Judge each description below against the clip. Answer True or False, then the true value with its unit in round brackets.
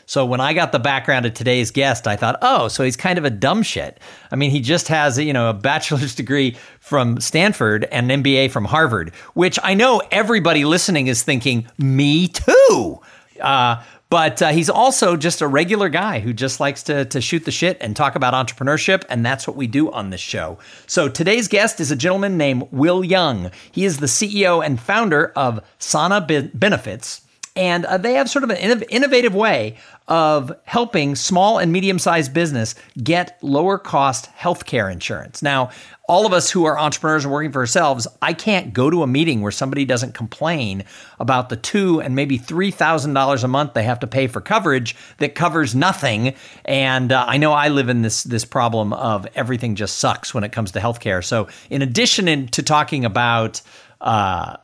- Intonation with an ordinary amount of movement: False (5.7 semitones)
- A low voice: False (145 Hz)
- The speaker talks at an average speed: True (195 wpm)